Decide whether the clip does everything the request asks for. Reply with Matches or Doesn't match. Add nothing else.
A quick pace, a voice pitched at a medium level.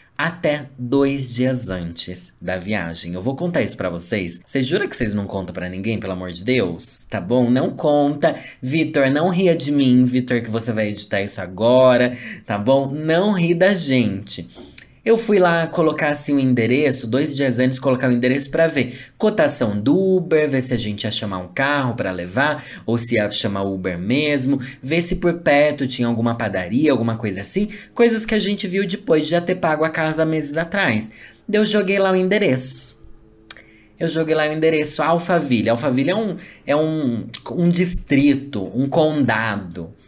Doesn't match